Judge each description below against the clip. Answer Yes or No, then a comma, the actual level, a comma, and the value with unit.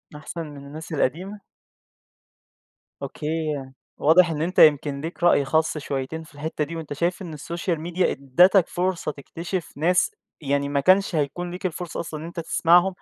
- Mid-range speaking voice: Yes, medium, 160 Hz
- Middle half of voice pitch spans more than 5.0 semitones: No, average, 3.2 semitones